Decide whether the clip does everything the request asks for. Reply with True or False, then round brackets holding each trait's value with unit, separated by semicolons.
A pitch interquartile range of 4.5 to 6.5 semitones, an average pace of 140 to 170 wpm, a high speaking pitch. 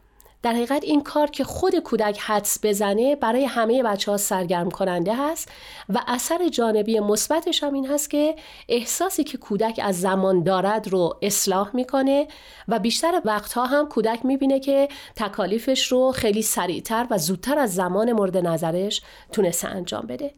True (5.3 semitones; 155 wpm; 230 Hz)